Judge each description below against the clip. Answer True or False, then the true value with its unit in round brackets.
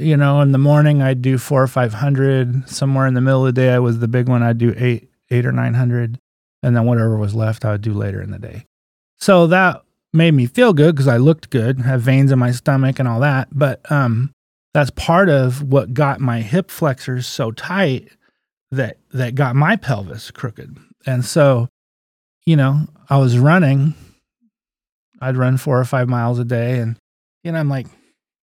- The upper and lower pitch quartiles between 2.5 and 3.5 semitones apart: True (3.1 semitones)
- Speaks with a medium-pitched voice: False (130 Hz)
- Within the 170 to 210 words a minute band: True (205 wpm)